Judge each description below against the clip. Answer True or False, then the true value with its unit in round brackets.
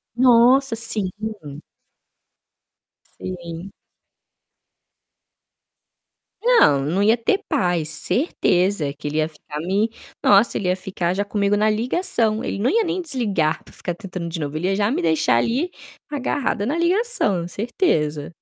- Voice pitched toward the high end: True (200 Hz)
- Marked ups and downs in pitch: True (6.4 semitones)